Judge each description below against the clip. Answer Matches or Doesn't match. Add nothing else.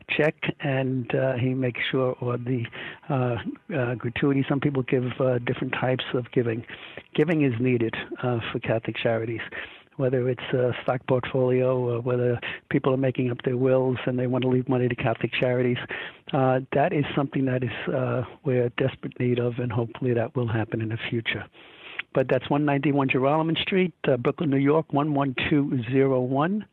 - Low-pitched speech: Matches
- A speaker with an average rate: Matches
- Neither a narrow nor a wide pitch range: Doesn't match